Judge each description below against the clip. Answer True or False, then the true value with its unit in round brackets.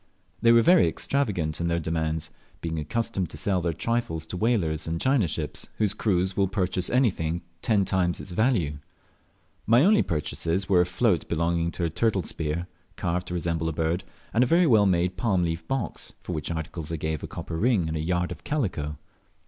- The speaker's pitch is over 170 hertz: False (90 Hz)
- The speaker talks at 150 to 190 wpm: False (200 wpm)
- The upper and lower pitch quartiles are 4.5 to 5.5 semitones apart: True (4.9 semitones)